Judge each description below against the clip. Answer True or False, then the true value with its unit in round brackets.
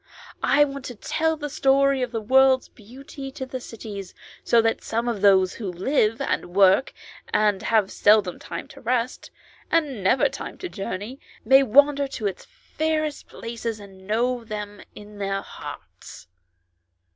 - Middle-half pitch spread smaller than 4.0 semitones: False (4.7 semitones)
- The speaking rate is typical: True (155 wpm)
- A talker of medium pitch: False (230 Hz)